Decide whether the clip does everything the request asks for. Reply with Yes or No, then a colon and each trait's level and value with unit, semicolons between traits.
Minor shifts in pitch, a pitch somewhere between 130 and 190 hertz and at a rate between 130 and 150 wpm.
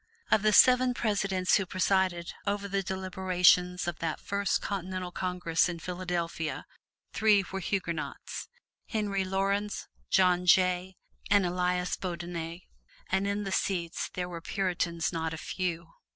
Yes: narrow, 2.0 semitones; medium, 185 Hz; slow, 135 wpm